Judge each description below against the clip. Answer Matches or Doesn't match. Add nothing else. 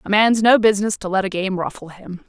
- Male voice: Doesn't match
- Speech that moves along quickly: Matches